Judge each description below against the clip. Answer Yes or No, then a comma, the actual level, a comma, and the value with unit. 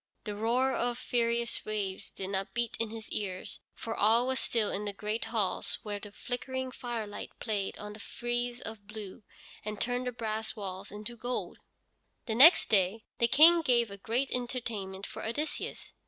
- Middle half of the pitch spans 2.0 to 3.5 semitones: Yes, average, 2.8 semitones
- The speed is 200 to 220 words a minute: No, average, 170 wpm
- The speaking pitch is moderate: No, high, 225 Hz